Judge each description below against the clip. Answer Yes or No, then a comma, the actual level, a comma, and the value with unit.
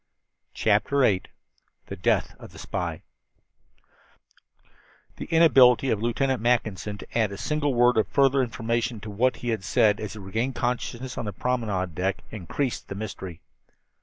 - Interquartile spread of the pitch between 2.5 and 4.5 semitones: Yes, average, 3.6 semitones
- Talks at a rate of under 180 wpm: Yes, average, 155 wpm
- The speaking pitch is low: Yes, low, 115 Hz